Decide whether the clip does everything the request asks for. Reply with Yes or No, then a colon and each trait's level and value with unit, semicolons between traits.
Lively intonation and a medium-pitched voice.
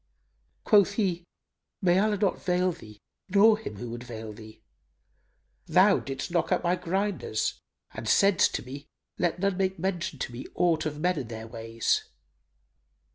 Yes: wide, 7.8 semitones; medium, 175 Hz